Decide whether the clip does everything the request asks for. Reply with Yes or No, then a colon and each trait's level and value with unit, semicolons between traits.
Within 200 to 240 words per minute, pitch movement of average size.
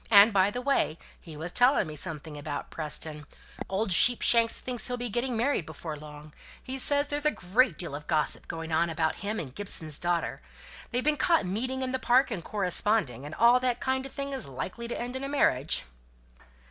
No: fast, 205 wpm; wide, 8.2 semitones